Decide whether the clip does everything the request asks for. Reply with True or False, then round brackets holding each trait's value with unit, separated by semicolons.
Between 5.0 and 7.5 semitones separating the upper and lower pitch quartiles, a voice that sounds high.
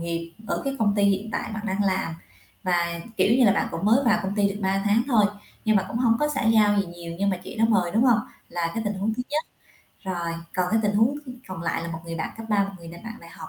False (4.2 semitones; 205 Hz)